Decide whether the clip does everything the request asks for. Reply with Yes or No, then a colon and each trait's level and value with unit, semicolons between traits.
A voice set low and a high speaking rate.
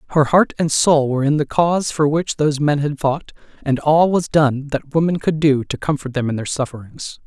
No: medium, 145 Hz; fast, 230 wpm